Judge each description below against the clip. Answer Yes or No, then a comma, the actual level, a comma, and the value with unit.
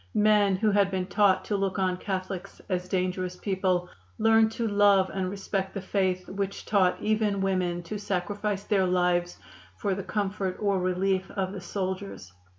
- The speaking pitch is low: No, high, 190 Hz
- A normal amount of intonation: No, narrow, 1.7 semitones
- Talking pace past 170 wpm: No, average, 165 wpm